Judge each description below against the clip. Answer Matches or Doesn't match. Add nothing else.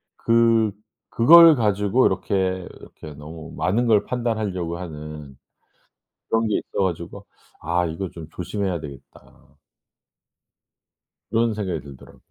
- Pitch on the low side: Matches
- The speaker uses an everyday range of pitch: Doesn't match